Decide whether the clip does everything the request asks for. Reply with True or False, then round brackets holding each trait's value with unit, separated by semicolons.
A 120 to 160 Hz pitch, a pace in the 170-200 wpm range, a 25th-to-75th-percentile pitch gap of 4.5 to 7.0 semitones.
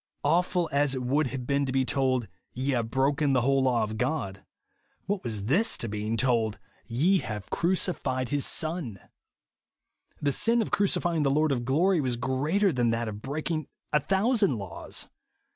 True (135 Hz; 185 wpm; 5.0 semitones)